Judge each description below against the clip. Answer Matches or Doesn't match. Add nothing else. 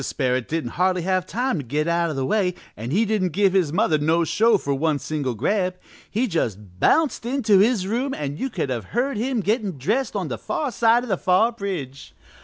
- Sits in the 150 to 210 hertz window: Matches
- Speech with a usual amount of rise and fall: Doesn't match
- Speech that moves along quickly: Matches